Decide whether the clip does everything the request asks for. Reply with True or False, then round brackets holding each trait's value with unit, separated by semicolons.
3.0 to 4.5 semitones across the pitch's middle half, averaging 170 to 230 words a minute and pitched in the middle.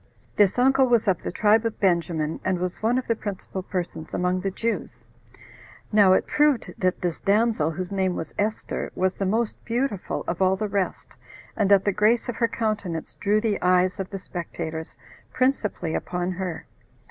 False (3.4 semitones; 180 wpm; 195 Hz)